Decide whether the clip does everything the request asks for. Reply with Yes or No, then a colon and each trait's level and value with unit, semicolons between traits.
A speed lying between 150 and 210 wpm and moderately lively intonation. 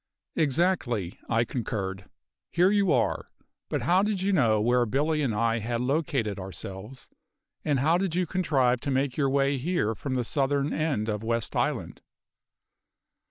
No: average, 160 wpm; wide, 5.8 semitones